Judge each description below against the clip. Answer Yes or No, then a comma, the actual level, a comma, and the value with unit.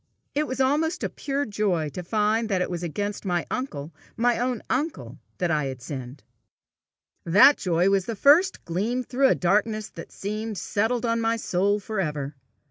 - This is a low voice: No, high, 210 Hz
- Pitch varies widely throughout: Yes, wide, 5.8 semitones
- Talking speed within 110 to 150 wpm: No, average, 185 wpm